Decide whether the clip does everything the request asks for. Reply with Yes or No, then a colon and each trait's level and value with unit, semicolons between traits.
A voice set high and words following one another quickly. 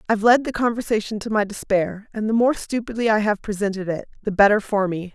Yes: high, 210 Hz; fast, 220 wpm